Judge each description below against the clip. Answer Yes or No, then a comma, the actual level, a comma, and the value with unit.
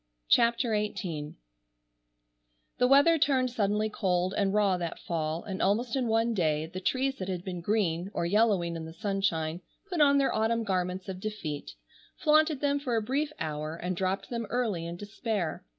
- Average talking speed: Yes, average, 175 wpm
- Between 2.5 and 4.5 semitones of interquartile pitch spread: No, average, 5.3 semitones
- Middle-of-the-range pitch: No, high, 205 Hz